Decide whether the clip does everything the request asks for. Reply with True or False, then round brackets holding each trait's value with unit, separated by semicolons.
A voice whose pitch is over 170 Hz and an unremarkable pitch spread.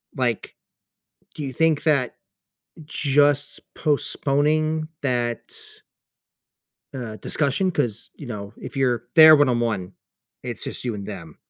False (135 Hz; 4.0 semitones)